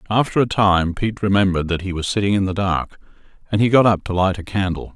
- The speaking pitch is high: No, low, 100 Hz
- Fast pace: Yes, fast, 240 wpm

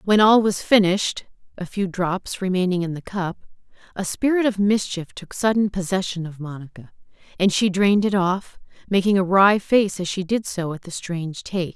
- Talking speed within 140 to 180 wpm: No, average, 190 wpm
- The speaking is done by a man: No, female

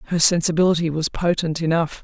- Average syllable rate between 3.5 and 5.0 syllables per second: No, 6.2 syllables/s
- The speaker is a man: No, female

